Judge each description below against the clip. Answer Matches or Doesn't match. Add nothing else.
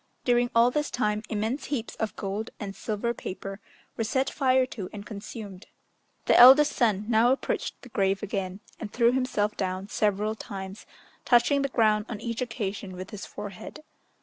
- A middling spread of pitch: Matches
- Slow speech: Doesn't match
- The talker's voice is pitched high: Matches